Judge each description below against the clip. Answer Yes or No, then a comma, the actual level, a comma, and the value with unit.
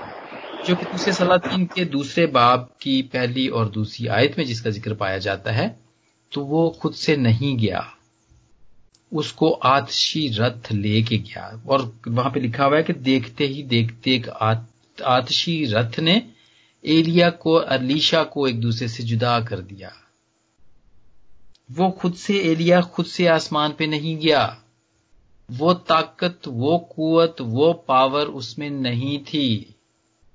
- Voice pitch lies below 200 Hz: Yes, low, 135 Hz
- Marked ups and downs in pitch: Yes, wide, 6.2 semitones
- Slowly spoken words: No, average, 140 wpm